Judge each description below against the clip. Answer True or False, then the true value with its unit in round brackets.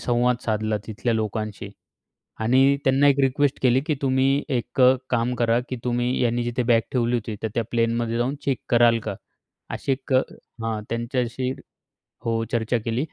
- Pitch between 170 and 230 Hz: False (120 Hz)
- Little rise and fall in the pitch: True (2.1 semitones)